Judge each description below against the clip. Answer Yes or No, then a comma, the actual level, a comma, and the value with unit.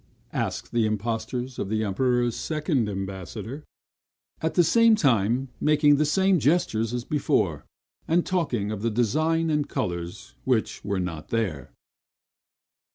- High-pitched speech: No, low, 120 Hz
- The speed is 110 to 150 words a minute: Yes, slow, 135 wpm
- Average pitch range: No, wide, 6.3 semitones